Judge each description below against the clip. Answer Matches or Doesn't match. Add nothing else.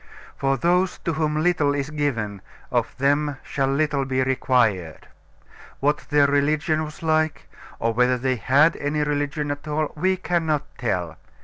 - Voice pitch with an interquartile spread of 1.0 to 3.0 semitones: Matches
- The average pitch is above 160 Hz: Doesn't match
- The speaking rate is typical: Matches